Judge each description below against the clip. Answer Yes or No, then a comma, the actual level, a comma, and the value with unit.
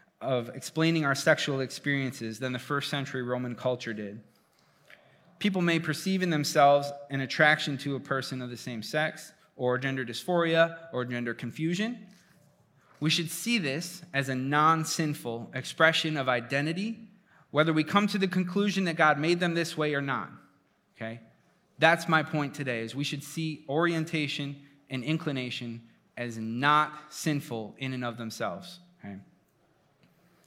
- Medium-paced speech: Yes, average, 150 wpm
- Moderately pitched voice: Yes, medium, 150 Hz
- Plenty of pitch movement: No, average, 4.2 semitones